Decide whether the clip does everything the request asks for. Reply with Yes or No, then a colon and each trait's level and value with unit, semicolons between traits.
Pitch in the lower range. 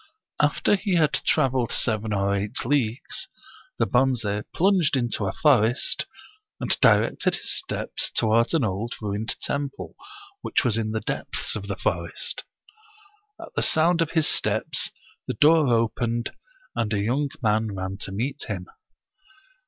Yes: low, 115 Hz